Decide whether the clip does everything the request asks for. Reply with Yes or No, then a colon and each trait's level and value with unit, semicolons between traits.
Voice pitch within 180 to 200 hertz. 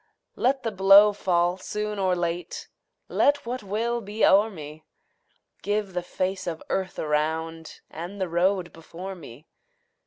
Yes: medium, 185 Hz